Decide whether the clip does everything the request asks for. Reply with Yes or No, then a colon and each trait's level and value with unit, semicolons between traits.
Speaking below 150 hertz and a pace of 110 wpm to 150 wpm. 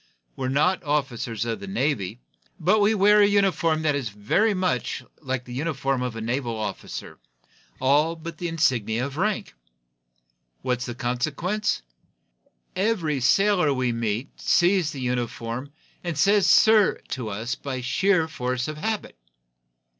Yes: medium, 140 Hz; average, 145 wpm